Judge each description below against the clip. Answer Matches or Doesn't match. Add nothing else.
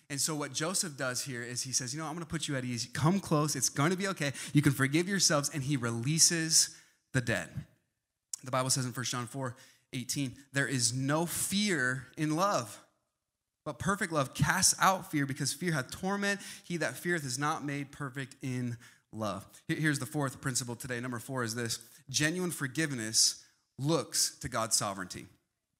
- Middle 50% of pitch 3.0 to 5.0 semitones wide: Matches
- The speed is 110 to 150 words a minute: Doesn't match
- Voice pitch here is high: Doesn't match